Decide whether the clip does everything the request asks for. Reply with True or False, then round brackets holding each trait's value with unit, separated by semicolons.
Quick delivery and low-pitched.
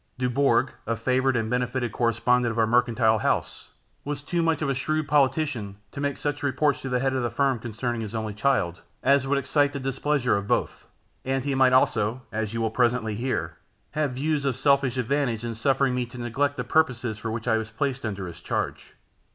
True (210 wpm; 125 Hz)